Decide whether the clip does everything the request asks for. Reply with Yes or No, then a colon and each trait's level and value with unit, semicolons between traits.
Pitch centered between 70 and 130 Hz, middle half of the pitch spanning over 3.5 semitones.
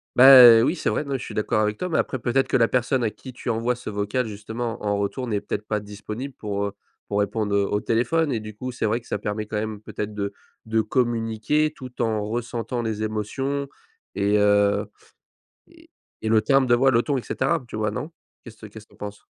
No: low, 110 Hz; average, 3.2 semitones